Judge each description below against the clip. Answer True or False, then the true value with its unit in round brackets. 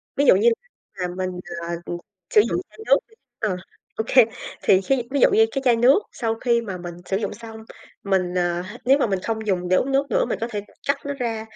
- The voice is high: True (220 Hz)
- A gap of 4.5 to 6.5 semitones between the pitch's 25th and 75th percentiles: True (5.1 semitones)